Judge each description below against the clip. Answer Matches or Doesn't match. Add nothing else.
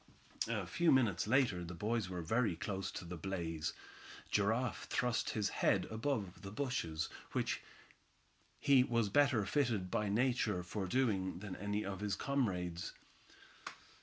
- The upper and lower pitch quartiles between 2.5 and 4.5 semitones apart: Doesn't match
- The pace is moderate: Matches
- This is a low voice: Matches